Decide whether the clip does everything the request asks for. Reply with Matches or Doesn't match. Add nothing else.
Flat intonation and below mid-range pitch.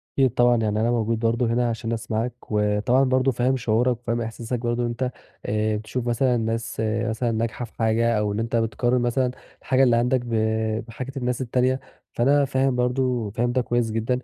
Matches